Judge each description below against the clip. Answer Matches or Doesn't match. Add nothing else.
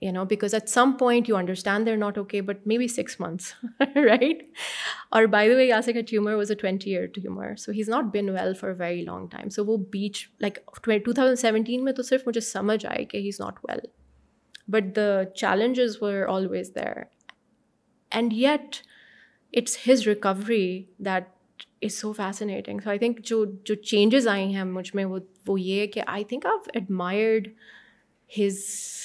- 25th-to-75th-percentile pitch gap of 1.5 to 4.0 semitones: Matches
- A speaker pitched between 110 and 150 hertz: Doesn't match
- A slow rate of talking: Doesn't match